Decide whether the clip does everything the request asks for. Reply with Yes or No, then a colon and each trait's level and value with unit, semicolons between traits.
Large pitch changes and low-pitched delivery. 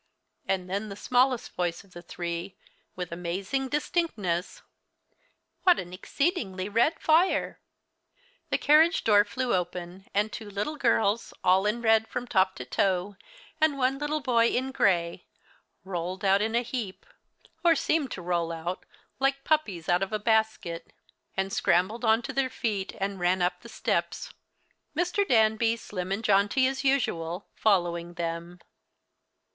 No: wide, 6.0 semitones; high, 205 Hz